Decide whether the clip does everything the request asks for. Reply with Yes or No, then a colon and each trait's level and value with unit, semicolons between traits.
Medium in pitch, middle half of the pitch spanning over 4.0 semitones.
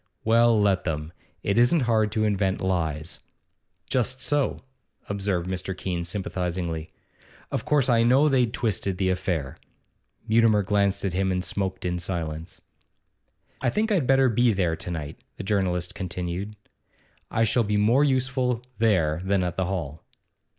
No: low, 100 Hz; average, 4.6 semitones